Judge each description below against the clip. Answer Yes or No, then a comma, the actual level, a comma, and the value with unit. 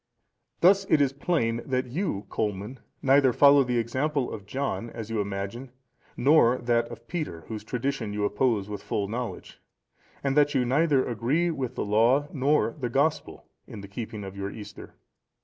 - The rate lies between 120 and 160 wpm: No, average, 175 wpm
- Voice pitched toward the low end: Yes, low, 120 Hz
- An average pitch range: Yes, average, 4.5 semitones